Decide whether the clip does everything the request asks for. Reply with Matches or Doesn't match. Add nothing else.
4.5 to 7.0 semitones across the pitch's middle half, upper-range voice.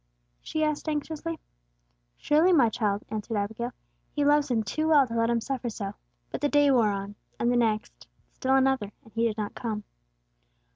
Matches